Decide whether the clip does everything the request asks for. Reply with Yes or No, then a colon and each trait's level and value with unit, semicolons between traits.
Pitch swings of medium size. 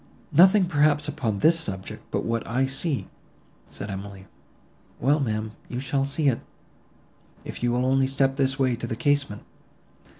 Yes: average, 4.0 semitones